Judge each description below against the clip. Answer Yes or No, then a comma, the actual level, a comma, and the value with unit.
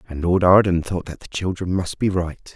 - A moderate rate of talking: No, fast, 235 wpm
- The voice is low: Yes, very low, 90 Hz